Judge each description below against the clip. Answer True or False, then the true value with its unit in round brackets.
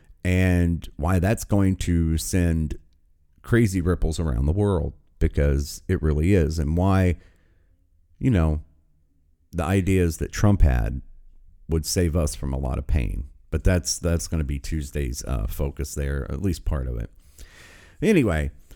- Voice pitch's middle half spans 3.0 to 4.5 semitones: True (3.4 semitones)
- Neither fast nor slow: True (155 wpm)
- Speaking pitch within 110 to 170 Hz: False (80 Hz)